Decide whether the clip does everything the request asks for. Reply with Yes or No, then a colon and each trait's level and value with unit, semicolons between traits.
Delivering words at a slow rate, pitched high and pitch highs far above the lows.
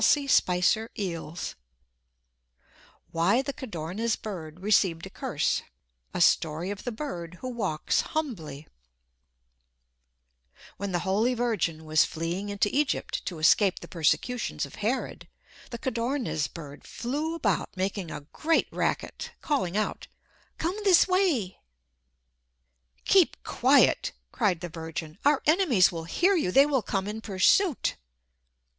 Yes: slow, 125 wpm; high, 205 Hz; wide, 7.6 semitones